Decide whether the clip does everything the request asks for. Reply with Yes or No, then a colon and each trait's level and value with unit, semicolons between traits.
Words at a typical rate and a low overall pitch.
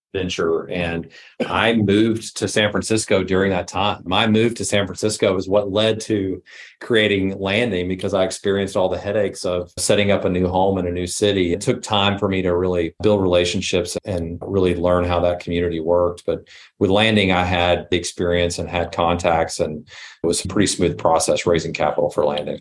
Yes: average, 195 wpm; very low, 95 Hz